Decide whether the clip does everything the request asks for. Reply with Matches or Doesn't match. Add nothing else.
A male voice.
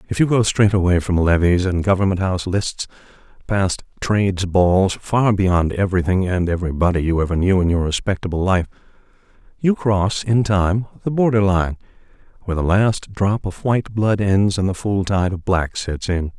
Matches